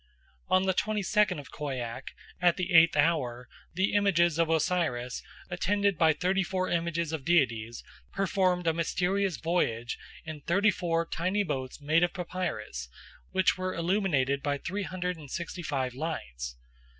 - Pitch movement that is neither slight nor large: Yes, average, 4.7 semitones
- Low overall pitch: No, medium, 170 Hz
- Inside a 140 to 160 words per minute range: Yes, average, 155 wpm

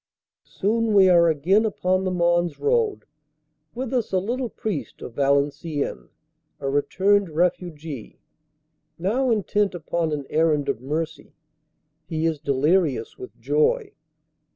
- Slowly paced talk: Yes, slow, 125 wpm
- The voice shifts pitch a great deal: Yes, wide, 5.7 semitones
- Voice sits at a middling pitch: Yes, medium, 175 Hz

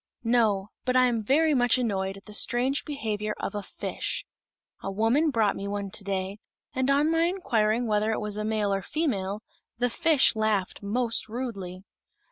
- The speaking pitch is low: No, high, 220 Hz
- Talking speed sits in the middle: Yes, average, 180 wpm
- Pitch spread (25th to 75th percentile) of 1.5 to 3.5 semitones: No, average, 3.9 semitones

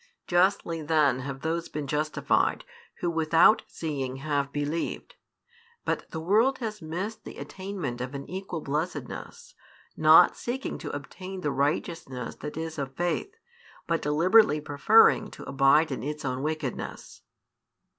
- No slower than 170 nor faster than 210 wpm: No, slow, 135 wpm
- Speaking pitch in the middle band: Yes, medium, 155 Hz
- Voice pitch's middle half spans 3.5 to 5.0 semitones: Yes, average, 4.0 semitones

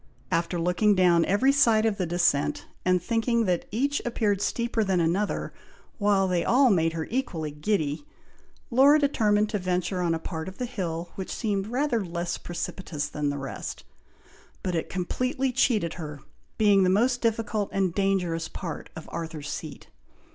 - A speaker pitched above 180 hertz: Yes, high, 190 Hz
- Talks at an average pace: Yes, average, 165 wpm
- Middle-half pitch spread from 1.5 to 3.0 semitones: No, average, 4.9 semitones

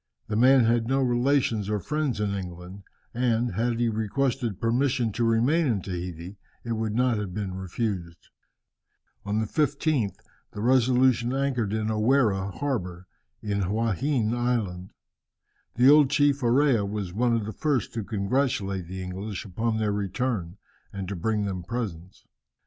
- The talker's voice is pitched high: No, low, 110 Hz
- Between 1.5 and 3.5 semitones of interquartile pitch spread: No, average, 4.1 semitones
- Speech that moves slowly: No, average, 155 wpm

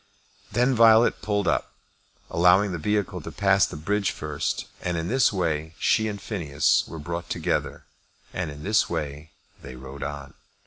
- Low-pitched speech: Yes, very low, 85 Hz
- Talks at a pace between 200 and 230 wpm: No, average, 165 wpm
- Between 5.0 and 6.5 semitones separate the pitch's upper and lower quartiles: Yes, wide, 5.5 semitones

